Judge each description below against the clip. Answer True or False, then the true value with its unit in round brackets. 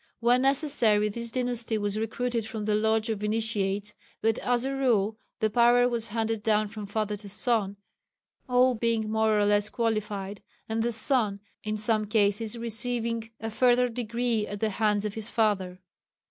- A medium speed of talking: True (170 wpm)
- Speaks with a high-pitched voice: True (220 Hz)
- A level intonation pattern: True (2.0 semitones)